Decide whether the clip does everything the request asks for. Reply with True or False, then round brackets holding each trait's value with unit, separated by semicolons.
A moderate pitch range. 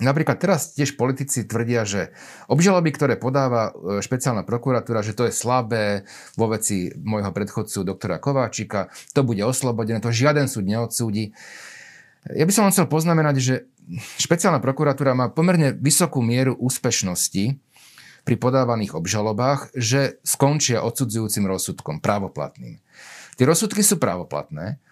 True (4.2 semitones)